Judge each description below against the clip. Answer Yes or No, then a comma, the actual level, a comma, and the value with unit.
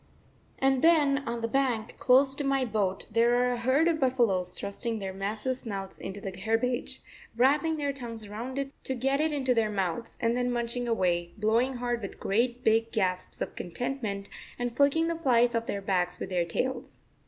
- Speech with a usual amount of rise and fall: Yes, average, 4.3 semitones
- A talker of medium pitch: No, high, 235 Hz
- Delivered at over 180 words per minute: Yes, average, 190 wpm